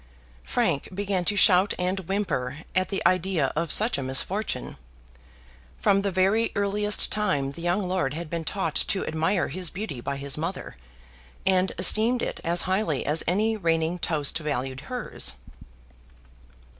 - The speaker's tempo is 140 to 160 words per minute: Yes, average, 150 wpm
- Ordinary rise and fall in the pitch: Yes, average, 4.6 semitones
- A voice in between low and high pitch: Yes, medium, 180 Hz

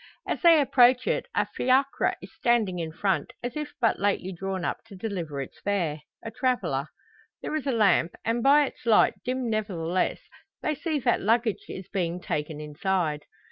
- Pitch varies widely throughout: Yes, wide, 6.2 semitones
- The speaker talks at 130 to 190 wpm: Yes, average, 180 wpm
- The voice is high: Yes, high, 205 Hz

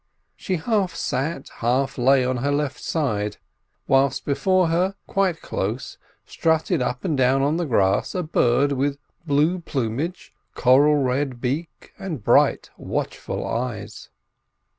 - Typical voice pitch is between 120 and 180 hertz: Yes, medium, 140 Hz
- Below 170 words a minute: Yes, slow, 135 wpm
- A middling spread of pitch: Yes, average, 4.6 semitones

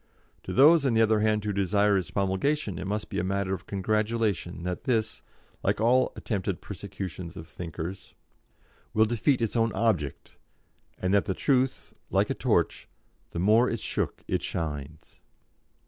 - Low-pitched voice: Yes, low, 105 Hz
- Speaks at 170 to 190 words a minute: No, average, 160 wpm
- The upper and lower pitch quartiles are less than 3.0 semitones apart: No, average, 3.7 semitones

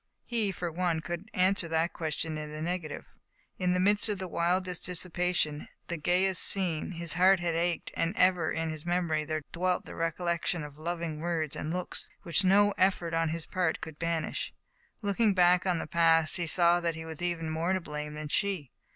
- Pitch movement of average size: No, narrow, 2.2 semitones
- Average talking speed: Yes, average, 195 wpm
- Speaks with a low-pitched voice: No, medium, 170 Hz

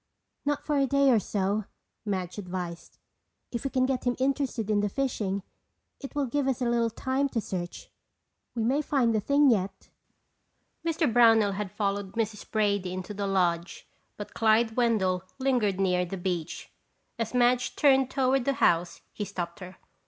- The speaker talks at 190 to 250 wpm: No, average, 170 wpm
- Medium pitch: No, high, 220 Hz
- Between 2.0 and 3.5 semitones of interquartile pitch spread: No, average, 5.3 semitones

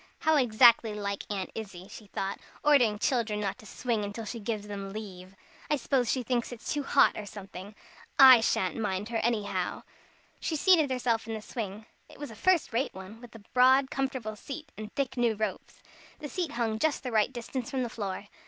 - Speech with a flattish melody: No, average, 3.8 semitones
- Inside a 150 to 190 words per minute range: No, fast, 205 wpm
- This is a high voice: Yes, high, 225 Hz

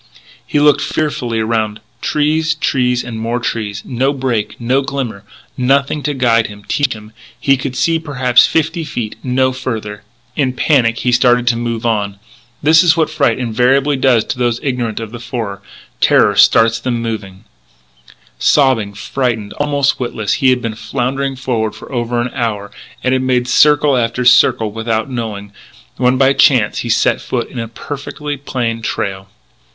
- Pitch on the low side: Yes, low, 125 Hz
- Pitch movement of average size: Yes, average, 3.3 semitones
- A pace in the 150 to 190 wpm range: Yes, average, 165 wpm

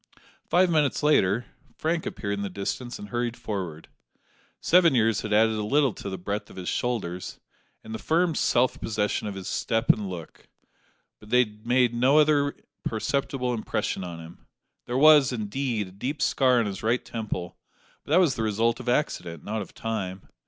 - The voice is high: No, low, 115 Hz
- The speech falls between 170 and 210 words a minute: Yes, average, 185 wpm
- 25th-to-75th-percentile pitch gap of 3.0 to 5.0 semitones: Yes, average, 4.6 semitones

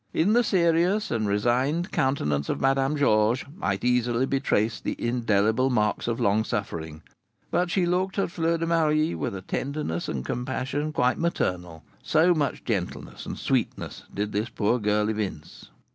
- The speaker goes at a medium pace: Yes, average, 160 wpm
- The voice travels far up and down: Yes, wide, 6.9 semitones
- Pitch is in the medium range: No, low, 125 Hz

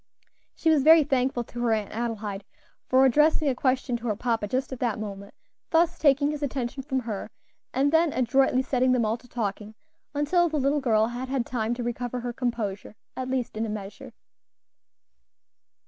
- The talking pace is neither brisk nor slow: Yes, average, 185 wpm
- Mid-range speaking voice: No, very high, 250 Hz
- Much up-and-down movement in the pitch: No, average, 3.3 semitones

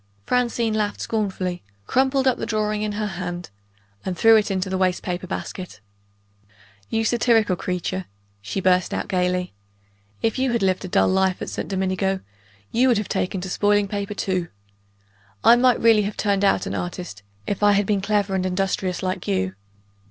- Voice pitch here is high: Yes, high, 195 Hz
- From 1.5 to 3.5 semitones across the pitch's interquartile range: Yes, narrow, 2.6 semitones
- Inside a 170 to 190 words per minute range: Yes, average, 180 wpm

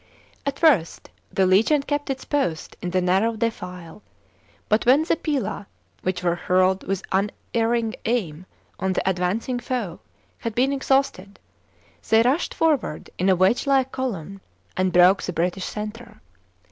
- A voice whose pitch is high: Yes, high, 210 Hz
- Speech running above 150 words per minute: No, average, 145 wpm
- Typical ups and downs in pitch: No, wide, 5.8 semitones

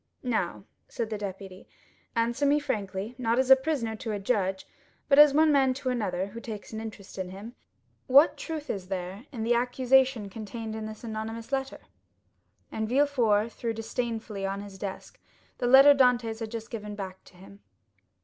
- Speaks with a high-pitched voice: Yes, high, 225 Hz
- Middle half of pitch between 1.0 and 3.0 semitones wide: No, average, 4.0 semitones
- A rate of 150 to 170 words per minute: No, average, 180 wpm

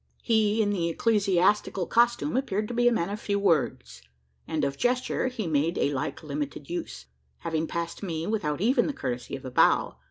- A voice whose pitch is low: No, medium, 175 Hz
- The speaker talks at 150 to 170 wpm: No, average, 190 wpm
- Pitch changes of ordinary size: No, wide, 6.6 semitones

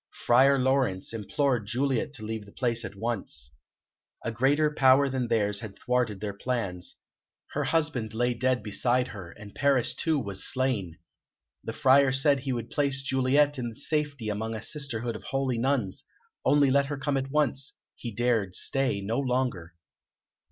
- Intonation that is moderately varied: Yes, average, 3.9 semitones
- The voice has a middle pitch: No, low, 125 Hz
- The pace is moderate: Yes, average, 165 wpm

